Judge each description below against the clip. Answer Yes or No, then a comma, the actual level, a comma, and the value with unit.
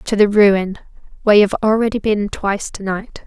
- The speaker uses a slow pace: No, average, 200 wpm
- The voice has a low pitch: No, high, 205 Hz